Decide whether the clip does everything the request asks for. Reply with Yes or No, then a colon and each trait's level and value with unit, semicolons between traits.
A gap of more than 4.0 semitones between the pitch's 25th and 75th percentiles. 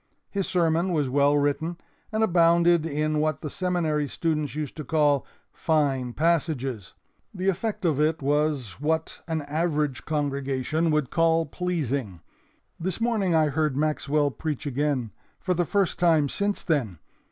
No: average, 2.9 semitones